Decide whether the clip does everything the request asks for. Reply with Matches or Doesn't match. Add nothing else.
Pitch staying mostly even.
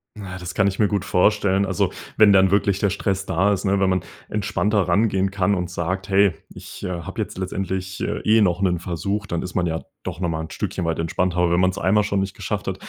Matches